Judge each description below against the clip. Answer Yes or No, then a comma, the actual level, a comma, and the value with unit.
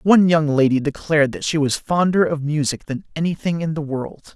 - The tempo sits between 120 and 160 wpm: No, fast, 205 wpm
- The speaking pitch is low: No, medium, 155 Hz